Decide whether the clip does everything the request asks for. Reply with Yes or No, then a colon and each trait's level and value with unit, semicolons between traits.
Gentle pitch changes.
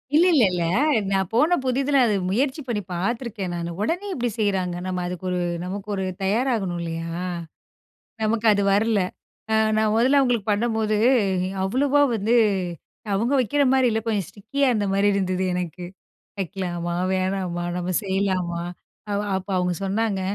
No: average, 4.3 semitones